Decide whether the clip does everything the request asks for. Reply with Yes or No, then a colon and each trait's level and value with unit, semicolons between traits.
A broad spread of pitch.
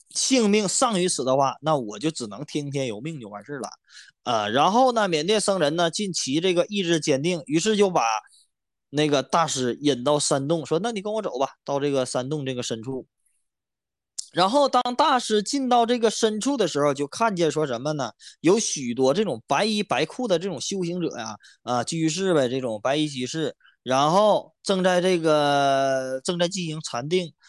Yes: wide, 6.1 semitones